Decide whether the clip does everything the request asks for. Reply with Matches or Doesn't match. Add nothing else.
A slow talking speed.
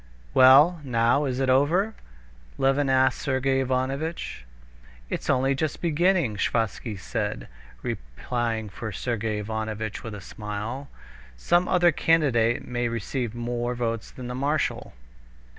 Matches